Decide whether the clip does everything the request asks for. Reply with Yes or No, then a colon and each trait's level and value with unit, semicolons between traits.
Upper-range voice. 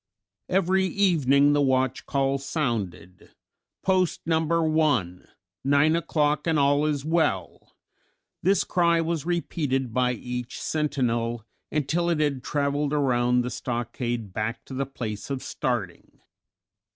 No: medium, 140 Hz